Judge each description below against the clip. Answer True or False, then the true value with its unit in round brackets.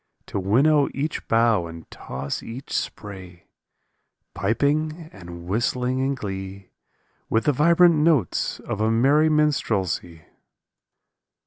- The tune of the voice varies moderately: False (7.5 semitones)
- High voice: False (115 Hz)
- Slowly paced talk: True (110 wpm)